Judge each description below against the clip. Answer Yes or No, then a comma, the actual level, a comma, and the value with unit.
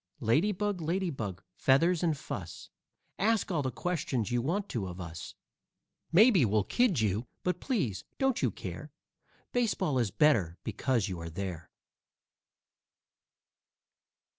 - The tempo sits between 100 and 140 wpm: Yes, slow, 135 wpm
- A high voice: No, low, 135 Hz